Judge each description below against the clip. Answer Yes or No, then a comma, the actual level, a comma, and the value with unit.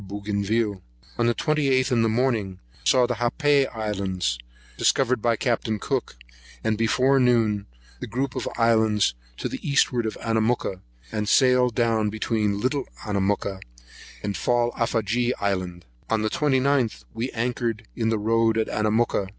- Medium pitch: No, low, 115 Hz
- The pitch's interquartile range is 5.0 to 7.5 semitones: No, average, 3.0 semitones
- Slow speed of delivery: No, average, 145 wpm